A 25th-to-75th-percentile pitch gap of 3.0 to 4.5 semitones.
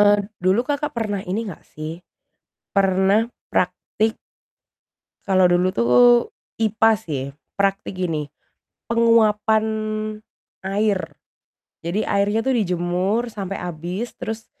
Yes: average, 3.5 semitones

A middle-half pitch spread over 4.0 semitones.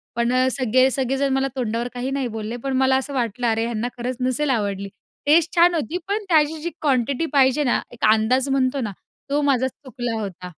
No: average, 2.9 semitones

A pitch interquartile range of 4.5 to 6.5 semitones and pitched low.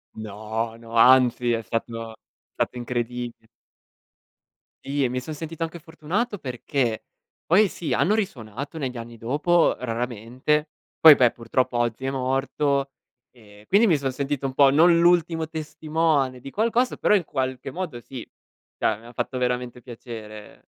Yes: average, 4.8 semitones; low, 130 Hz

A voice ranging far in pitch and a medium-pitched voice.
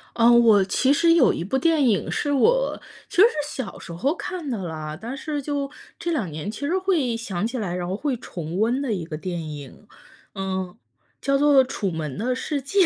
No: wide, 7.7 semitones; high, 235 Hz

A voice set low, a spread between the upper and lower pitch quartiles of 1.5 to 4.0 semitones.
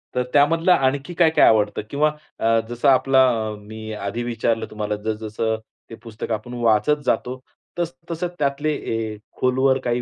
No: low, 120 Hz; average, 4.4 semitones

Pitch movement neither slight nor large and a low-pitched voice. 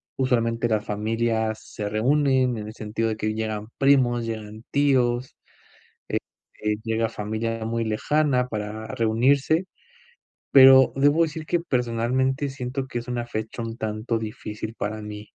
Yes: average, 3.2 semitones; low, 115 Hz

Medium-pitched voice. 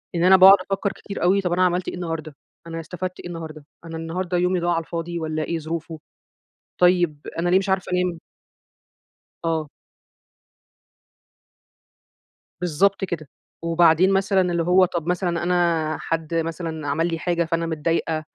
Yes: medium, 170 Hz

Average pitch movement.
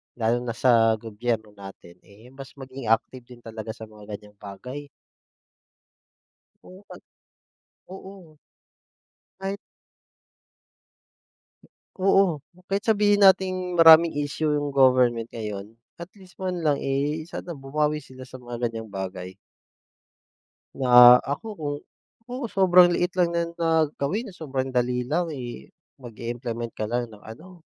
No: wide, 6.8 semitones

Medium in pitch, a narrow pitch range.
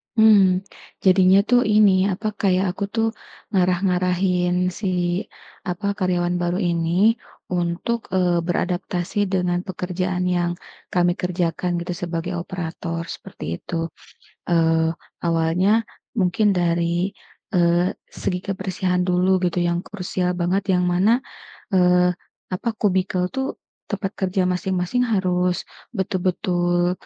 Yes: medium, 180 Hz; narrow, 1.5 semitones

